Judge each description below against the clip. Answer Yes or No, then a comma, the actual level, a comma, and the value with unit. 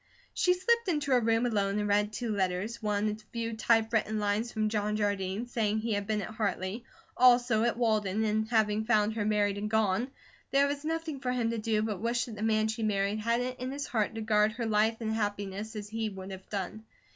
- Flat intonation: Yes, narrow, 2.1 semitones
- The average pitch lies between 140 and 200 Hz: No, high, 220 Hz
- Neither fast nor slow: No, fast, 225 wpm